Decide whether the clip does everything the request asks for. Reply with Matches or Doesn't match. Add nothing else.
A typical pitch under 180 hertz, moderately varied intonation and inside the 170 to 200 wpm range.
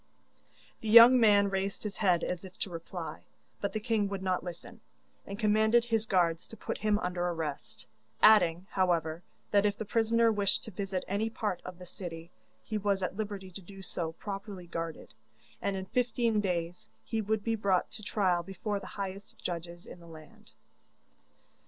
Doesn't match